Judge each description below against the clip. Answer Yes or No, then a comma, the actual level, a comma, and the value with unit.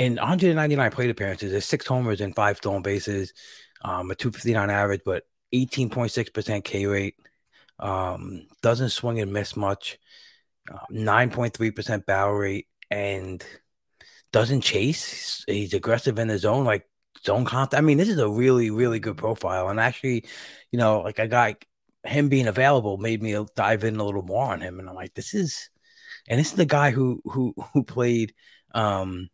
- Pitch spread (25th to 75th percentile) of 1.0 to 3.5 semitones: No, average, 3.9 semitones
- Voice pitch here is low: Yes, low, 110 Hz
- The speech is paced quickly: No, average, 170 wpm